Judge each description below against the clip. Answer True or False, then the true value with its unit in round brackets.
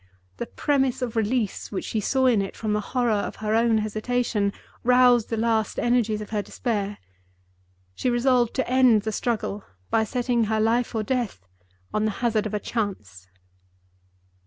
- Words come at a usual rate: True (170 wpm)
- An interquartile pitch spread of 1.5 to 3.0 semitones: True (2.7 semitones)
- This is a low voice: False (225 Hz)